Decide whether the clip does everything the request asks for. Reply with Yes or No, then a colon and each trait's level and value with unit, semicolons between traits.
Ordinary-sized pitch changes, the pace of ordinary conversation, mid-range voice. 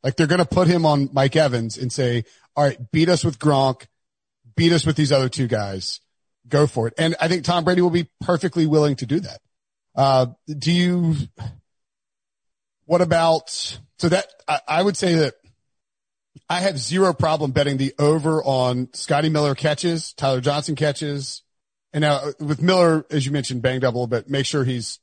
Yes: average, 4.0 semitones; average, 185 wpm; medium, 145 Hz